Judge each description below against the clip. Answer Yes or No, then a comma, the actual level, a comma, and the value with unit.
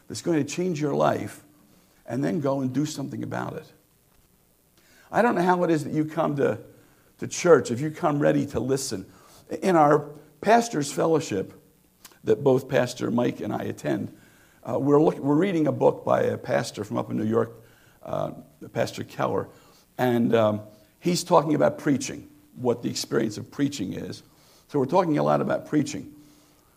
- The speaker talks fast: No, average, 180 wpm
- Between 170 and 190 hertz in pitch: No, medium, 140 Hz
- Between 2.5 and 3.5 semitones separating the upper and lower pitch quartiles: No, average, 5.0 semitones